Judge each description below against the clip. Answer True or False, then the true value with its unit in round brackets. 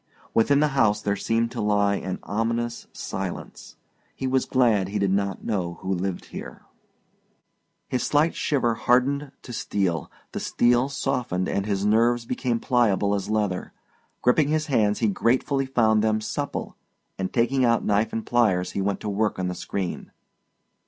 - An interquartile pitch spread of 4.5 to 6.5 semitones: False (3.7 semitones)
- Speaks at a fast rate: False (165 wpm)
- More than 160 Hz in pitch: False (110 Hz)